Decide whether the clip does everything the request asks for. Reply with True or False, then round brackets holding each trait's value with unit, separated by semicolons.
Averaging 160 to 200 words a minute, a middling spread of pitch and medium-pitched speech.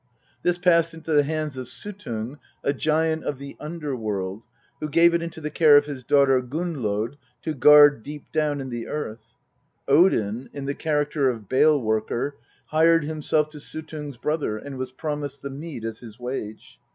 True (175 wpm; 3.8 semitones; 145 Hz)